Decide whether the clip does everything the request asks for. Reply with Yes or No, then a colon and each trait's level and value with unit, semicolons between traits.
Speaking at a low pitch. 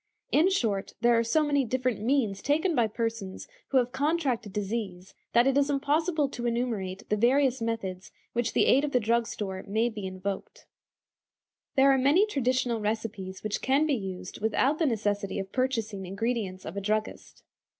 No: high, 230 Hz